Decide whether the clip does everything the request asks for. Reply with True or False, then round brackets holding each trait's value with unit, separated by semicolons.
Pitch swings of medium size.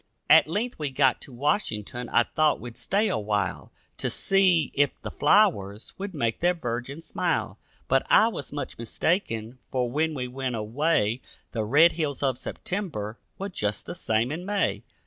False (6.4 semitones)